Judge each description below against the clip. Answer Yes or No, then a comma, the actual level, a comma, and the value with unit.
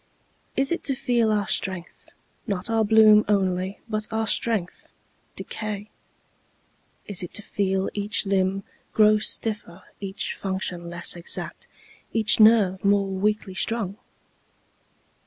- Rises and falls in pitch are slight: Yes, narrow, 2.3 semitones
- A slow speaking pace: Yes, slow, 120 wpm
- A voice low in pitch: No, high, 205 Hz